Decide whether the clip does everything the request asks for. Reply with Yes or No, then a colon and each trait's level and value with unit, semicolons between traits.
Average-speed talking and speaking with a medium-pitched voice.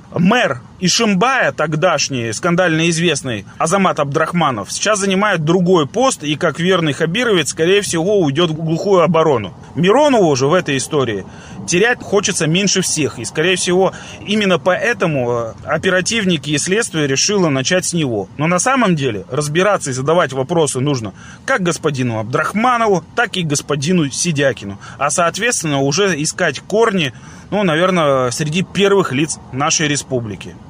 Yes: average, 135 wpm; medium, 165 Hz